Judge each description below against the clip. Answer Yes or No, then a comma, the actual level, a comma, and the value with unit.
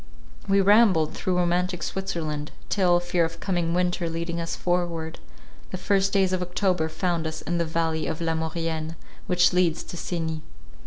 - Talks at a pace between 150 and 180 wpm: Yes, average, 165 wpm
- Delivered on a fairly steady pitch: Yes, narrow, 1.8 semitones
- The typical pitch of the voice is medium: Yes, medium, 175 Hz